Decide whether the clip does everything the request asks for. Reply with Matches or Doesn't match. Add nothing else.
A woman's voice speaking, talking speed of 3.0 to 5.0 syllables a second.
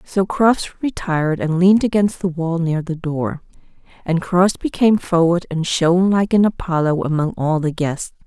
Matches